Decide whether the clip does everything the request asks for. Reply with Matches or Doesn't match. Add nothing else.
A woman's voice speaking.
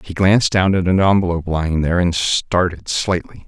Doesn't match